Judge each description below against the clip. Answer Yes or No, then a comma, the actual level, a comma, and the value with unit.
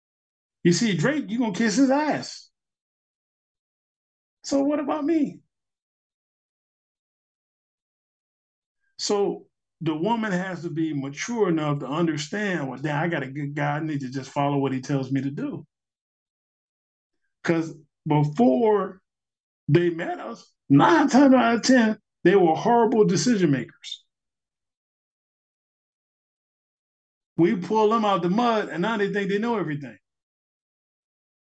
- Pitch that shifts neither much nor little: No, wide, 8.0 semitones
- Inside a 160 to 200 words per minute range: No, slow, 135 wpm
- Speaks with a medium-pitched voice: Yes, medium, 180 Hz